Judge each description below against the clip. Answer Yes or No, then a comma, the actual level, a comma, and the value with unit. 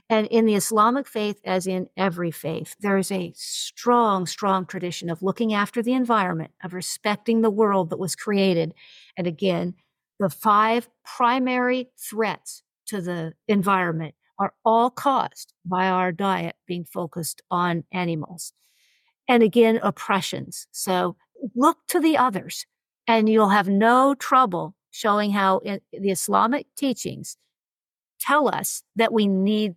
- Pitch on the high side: Yes, high, 200 Hz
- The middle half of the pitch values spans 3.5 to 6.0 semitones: Yes, average, 4.1 semitones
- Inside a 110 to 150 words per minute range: Yes, average, 140 wpm